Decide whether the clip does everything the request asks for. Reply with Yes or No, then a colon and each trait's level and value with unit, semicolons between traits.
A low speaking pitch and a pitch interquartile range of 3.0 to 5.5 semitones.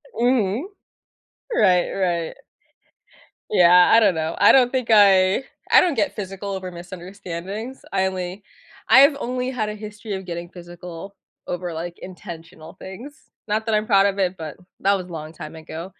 No: high, 190 Hz; average, 3.5 semitones